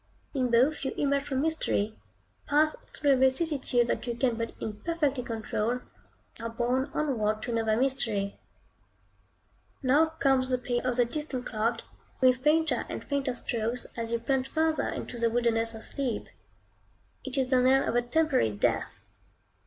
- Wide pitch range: No, average, 3.1 semitones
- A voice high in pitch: Yes, very high, 255 Hz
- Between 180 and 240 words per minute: No, average, 160 wpm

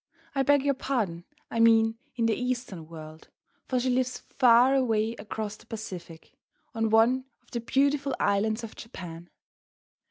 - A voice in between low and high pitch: No, high, 225 Hz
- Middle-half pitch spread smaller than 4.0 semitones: Yes, average, 3.6 semitones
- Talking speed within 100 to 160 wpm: Yes, average, 155 wpm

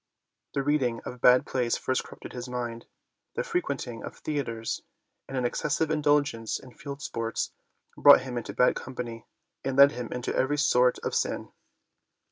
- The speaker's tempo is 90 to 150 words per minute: No, average, 165 wpm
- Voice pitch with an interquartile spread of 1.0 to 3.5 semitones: Yes, average, 2.9 semitones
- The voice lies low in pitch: Yes, low, 125 Hz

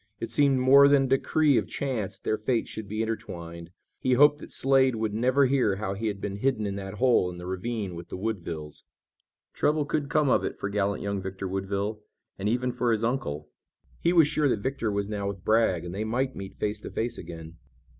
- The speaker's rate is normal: No, fast, 225 wpm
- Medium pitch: No, low, 110 Hz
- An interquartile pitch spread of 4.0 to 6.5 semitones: Yes, average, 5.0 semitones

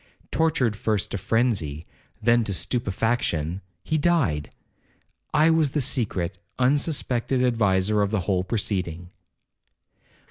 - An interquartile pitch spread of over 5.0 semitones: Yes, wide, 5.6 semitones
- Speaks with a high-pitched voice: No, low, 110 Hz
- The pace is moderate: No, slow, 105 wpm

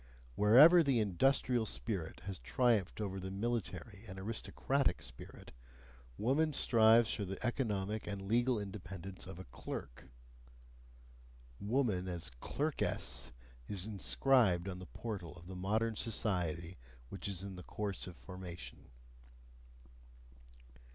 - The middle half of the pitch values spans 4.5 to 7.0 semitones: No, average, 4.1 semitones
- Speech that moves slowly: Yes, slow, 115 wpm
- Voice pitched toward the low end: Yes, low, 100 Hz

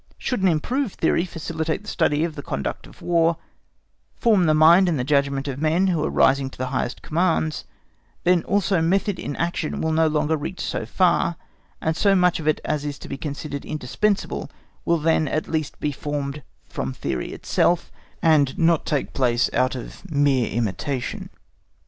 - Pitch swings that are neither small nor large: Yes, average, 3.4 semitones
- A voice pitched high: No, medium, 155 Hz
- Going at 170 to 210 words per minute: Yes, average, 180 wpm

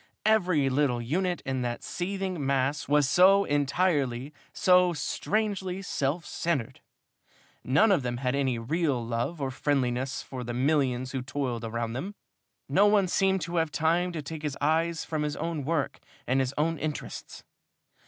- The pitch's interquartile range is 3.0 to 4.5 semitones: No, average, 5.1 semitones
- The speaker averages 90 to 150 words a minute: No, average, 160 wpm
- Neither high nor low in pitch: Yes, medium, 145 Hz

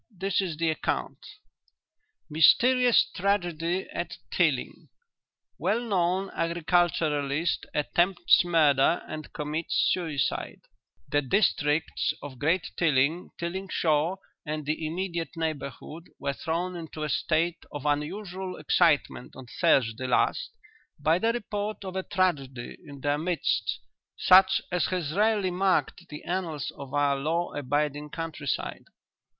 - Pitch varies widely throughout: No, average, 3.8 semitones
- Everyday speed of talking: No, slow, 120 wpm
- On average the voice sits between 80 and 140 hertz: No, medium, 165 Hz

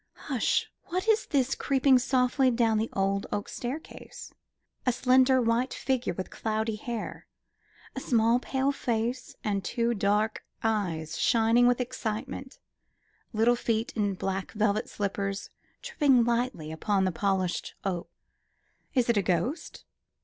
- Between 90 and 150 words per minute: Yes, slow, 135 wpm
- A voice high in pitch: Yes, high, 230 Hz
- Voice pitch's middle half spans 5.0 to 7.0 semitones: No, average, 4.0 semitones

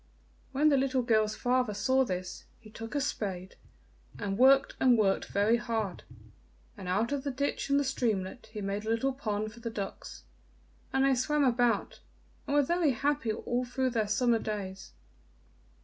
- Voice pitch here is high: Yes, high, 235 Hz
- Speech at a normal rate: Yes, average, 175 wpm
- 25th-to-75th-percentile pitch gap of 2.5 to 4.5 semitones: Yes, average, 4.1 semitones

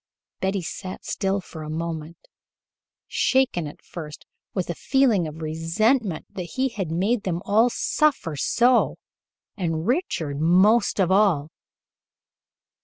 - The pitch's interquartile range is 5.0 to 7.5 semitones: Yes, wide, 5.4 semitones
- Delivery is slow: Yes, slow, 125 wpm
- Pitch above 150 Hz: Yes, medium, 185 Hz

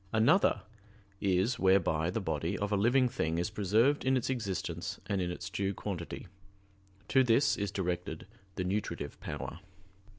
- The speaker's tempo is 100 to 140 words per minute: No, average, 155 wpm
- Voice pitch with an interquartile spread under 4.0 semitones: No, average, 4.4 semitones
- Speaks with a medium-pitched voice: No, low, 100 Hz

